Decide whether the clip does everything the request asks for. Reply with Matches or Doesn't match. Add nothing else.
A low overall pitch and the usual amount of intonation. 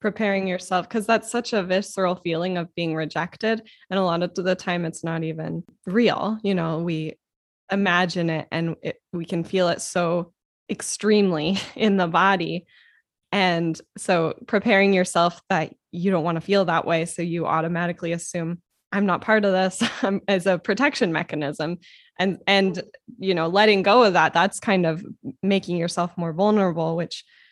Doesn't match